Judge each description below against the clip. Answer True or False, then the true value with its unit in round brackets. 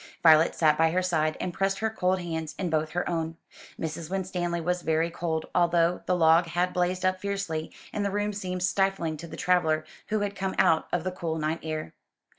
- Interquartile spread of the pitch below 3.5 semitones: True (2.5 semitones)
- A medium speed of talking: False (210 wpm)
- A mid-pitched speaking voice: True (175 Hz)